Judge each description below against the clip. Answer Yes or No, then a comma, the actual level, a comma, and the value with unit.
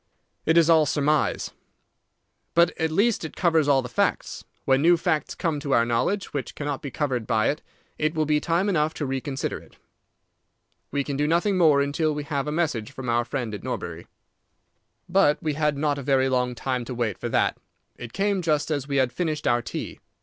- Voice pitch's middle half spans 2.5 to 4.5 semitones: Yes, average, 3.3 semitones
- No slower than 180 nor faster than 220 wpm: Yes, fast, 205 wpm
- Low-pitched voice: No, medium, 145 Hz